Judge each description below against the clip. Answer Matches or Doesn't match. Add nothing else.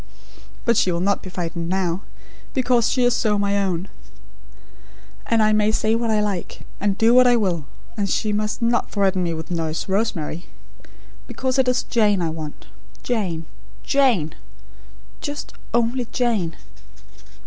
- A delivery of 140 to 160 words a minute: Matches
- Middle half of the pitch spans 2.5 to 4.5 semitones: Doesn't match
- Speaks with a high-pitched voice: Matches